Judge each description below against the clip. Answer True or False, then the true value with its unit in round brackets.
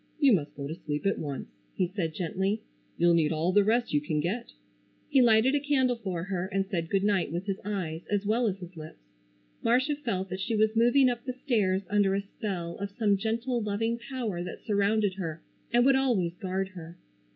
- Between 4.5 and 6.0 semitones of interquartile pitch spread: True (4.8 semitones)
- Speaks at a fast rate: True (210 wpm)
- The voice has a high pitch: True (200 Hz)